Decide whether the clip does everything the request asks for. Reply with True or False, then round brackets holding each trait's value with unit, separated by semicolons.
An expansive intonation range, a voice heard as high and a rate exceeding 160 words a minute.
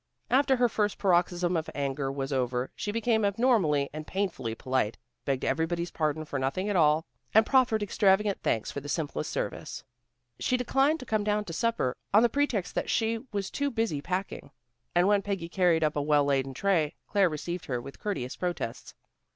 False (6.4 semitones; 180 Hz; 185 wpm)